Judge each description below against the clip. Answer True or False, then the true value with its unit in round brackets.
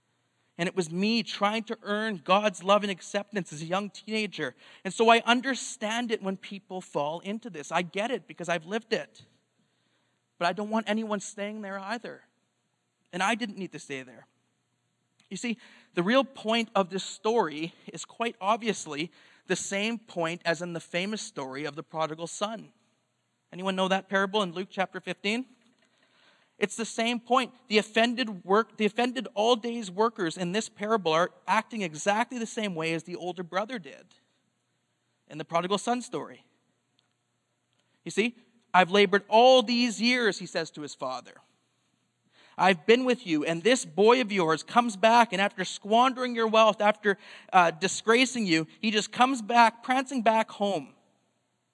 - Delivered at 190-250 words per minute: False (170 wpm)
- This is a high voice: True (205 Hz)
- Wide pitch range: False (4.3 semitones)